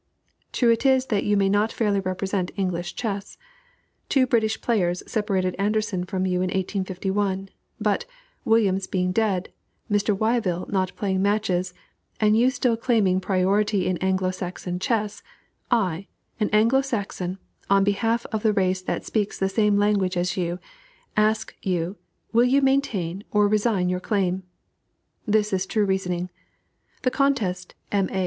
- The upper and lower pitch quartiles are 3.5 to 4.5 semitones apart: No, average, 2.8 semitones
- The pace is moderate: Yes, average, 145 wpm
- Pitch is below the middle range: No, high, 200 Hz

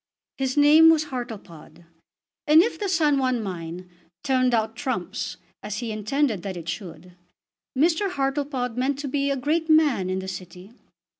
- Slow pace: No, average, 160 wpm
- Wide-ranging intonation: Yes, wide, 7.2 semitones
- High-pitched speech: Yes, very high, 255 Hz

